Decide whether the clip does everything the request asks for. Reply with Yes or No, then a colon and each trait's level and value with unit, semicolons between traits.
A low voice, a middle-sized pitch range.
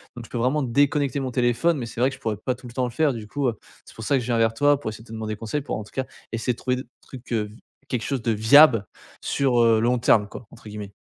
Yes: low, 120 Hz; average, 3.0 semitones